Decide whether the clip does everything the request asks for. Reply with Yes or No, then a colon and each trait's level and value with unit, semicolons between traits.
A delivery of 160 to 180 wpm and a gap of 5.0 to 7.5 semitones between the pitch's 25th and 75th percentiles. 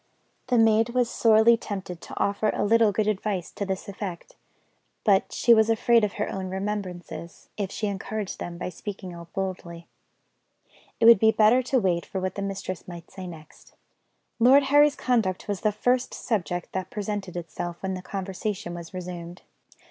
No: average, 175 wpm; average, 3.3 semitones